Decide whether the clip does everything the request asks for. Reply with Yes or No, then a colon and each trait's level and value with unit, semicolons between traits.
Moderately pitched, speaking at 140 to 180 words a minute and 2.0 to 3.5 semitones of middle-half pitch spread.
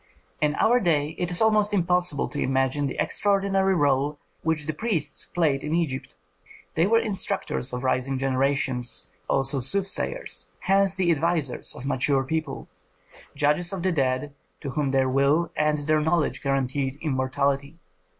No: medium, 150 Hz; average, 150 wpm; average, 4.5 semitones